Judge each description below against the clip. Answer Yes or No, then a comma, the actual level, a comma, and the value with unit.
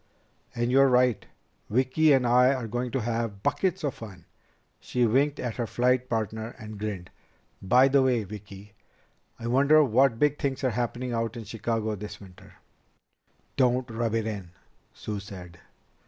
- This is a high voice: No, low, 120 Hz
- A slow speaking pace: No, average, 160 wpm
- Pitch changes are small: No, average, 3.2 semitones